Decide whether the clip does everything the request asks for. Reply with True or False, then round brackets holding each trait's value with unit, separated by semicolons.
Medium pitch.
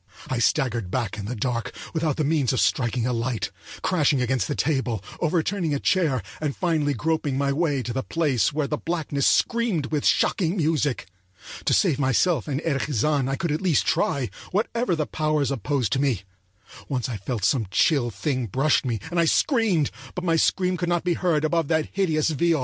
True (145 Hz)